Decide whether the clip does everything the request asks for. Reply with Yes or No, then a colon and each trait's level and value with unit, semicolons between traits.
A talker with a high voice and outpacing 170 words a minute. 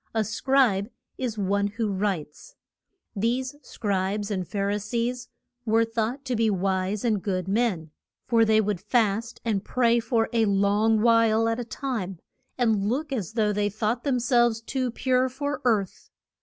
No: high, 220 Hz; average, 165 wpm